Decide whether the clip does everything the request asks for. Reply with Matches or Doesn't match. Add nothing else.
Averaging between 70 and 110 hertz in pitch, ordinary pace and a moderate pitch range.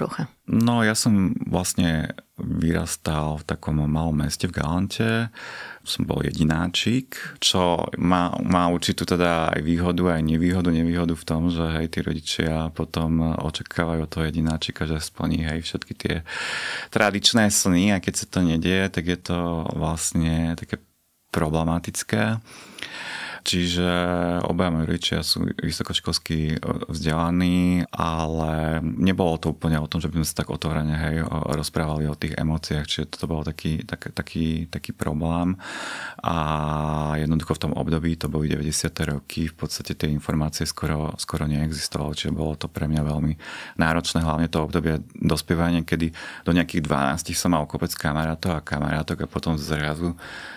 Doesn't match